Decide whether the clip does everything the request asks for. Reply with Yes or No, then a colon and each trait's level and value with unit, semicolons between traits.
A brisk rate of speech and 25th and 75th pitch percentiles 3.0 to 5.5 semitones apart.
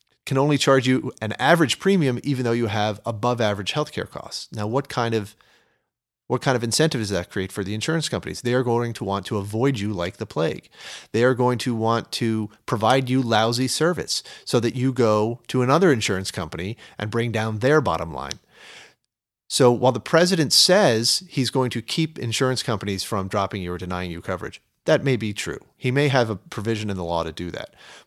Yes: fast, 210 wpm; average, 4.0 semitones